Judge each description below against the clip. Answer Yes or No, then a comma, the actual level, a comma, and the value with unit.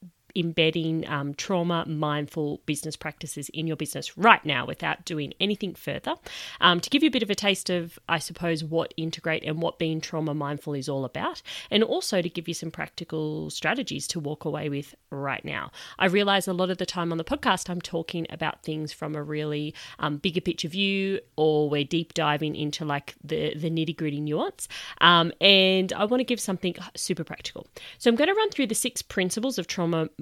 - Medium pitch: Yes, medium, 165 Hz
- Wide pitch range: No, average, 3.5 semitones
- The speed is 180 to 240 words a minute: Yes, fast, 205 wpm